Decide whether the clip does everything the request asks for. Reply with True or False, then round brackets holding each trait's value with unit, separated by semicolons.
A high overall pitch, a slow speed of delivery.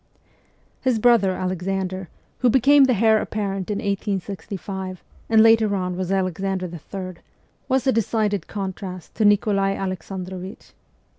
True (195 Hz; 125 wpm)